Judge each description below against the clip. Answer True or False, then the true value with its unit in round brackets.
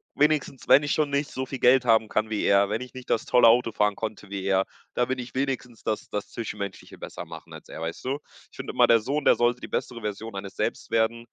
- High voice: False (115 Hz)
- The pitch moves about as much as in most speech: True (3.5 semitones)